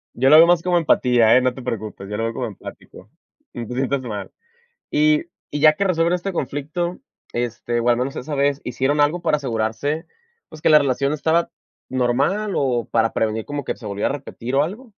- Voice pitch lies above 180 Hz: No, medium, 140 Hz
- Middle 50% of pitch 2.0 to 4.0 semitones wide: No, average, 5.0 semitones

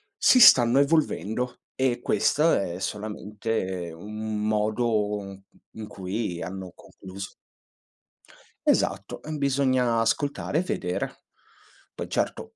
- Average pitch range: Yes, average, 4.4 semitones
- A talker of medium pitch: No, low, 110 Hz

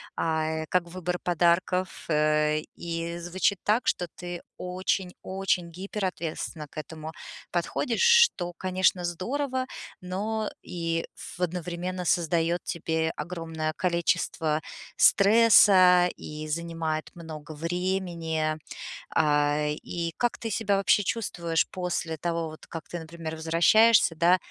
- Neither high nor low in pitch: Yes, medium, 170 Hz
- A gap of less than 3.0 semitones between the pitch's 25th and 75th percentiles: Yes, narrow, 2.4 semitones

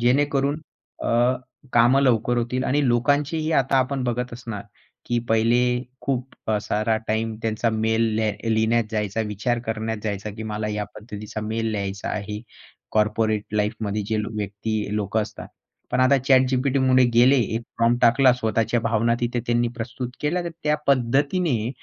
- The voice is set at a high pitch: No, low, 115 Hz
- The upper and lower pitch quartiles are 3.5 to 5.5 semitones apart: No, average, 2.8 semitones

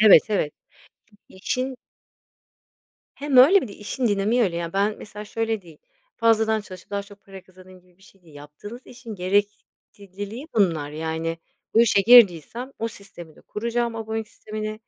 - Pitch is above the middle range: Yes, high, 205 Hz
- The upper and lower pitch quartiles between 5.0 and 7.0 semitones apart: No, average, 3.6 semitones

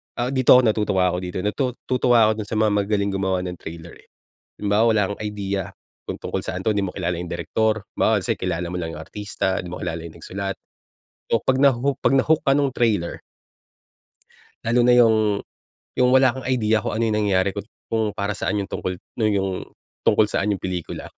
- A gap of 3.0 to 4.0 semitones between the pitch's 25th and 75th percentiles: Yes, average, 3.7 semitones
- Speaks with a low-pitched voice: Yes, low, 105 Hz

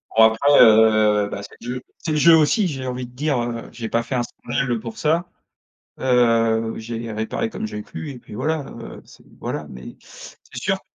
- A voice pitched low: Yes, low, 120 Hz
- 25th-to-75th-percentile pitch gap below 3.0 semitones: No, average, 3.5 semitones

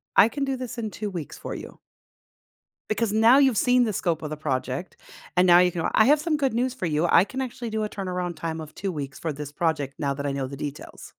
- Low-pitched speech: No, medium, 180 Hz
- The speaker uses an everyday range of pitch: No, wide, 7.4 semitones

